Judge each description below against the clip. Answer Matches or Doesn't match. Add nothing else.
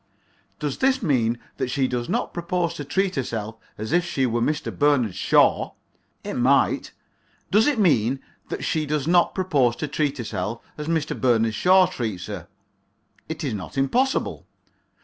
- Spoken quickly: Doesn't match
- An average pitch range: Doesn't match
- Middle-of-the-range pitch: Matches